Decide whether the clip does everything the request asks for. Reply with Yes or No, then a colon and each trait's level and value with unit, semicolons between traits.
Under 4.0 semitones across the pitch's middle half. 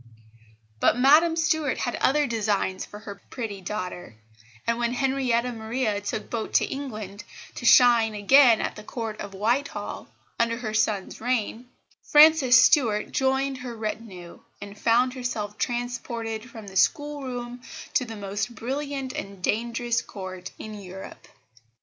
Yes: average, 3.5 semitones